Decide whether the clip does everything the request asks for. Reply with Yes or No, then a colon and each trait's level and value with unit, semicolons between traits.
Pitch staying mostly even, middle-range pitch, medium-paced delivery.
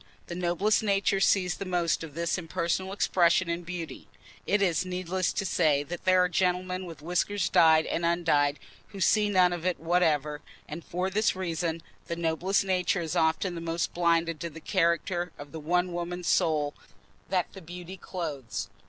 Yes: narrow, 2.0 semitones; medium, 175 Hz; average, 180 wpm